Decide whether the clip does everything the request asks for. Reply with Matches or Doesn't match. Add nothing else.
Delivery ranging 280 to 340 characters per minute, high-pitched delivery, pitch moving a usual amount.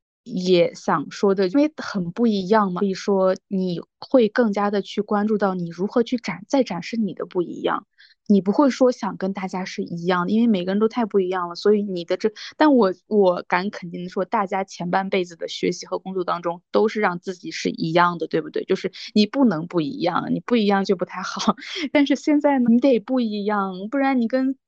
Matches